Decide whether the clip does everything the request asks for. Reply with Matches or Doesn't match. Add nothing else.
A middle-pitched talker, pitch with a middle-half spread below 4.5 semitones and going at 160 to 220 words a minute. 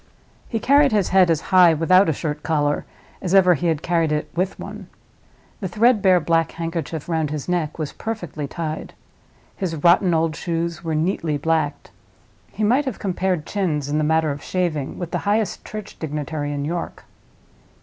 Matches